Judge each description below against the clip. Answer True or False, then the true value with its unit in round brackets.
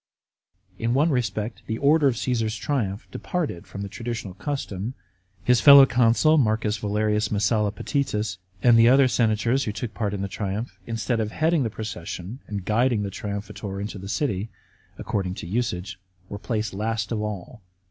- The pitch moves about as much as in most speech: True (3.3 semitones)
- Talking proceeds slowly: False (170 wpm)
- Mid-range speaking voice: False (110 Hz)